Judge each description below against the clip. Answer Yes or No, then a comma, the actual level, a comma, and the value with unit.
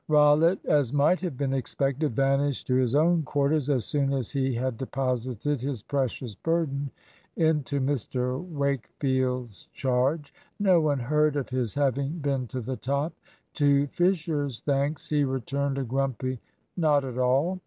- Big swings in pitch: No, narrow, 2.4 semitones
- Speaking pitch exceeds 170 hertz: No, medium, 140 Hz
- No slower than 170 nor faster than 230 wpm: No, average, 150 wpm